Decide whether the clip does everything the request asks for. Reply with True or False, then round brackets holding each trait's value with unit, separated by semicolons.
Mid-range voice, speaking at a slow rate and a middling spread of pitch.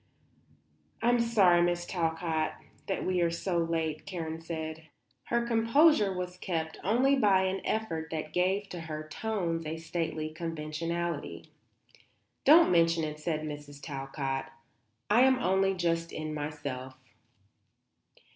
True (165 Hz; 125 wpm; 3.5 semitones)